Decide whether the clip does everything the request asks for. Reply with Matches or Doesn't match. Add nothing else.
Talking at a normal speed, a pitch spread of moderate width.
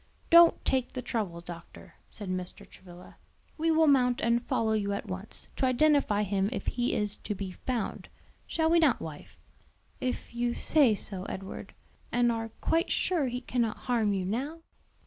Matches